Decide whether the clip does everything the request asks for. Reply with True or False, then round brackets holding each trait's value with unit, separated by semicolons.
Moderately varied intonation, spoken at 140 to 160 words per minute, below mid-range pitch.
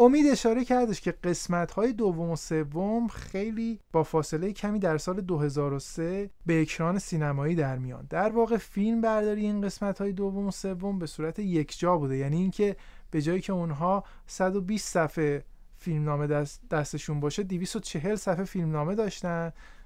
False (4.2 semitones; 155 wpm; 180 Hz)